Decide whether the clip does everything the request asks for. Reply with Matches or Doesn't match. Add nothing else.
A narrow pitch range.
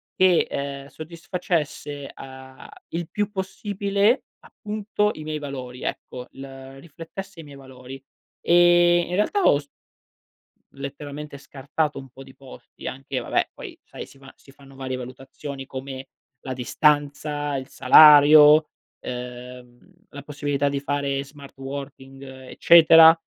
Doesn't match